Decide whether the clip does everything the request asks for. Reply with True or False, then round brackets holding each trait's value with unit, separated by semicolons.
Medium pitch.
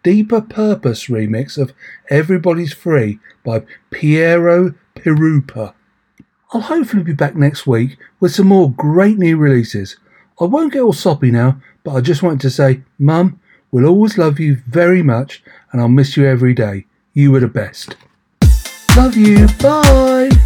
True (150 Hz)